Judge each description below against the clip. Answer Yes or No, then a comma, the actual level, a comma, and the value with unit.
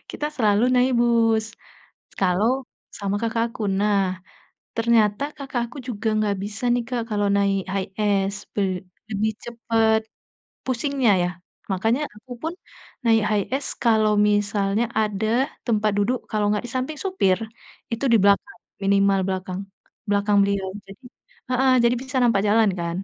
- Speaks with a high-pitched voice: Yes, high, 215 Hz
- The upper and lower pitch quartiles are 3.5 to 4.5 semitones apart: No, average, 2.9 semitones